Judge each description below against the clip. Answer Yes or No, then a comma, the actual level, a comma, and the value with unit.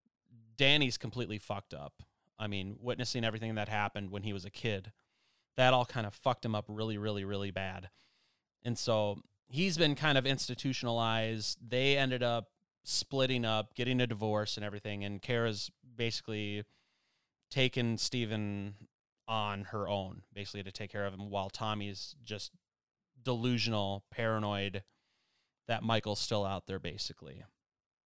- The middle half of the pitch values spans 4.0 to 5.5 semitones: No, average, 3.3 semitones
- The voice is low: Yes, low, 110 Hz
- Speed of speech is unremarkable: Yes, average, 145 wpm